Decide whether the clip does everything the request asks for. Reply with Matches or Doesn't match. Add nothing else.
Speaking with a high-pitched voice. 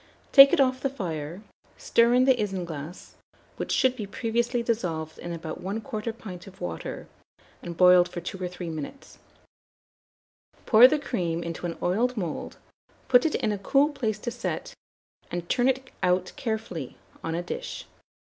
Matches